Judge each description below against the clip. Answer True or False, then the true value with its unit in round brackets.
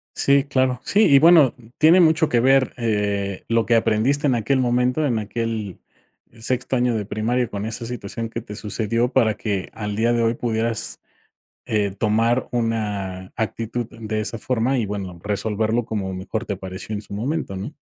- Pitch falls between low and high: False (115 Hz)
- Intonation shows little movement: False (3.0 semitones)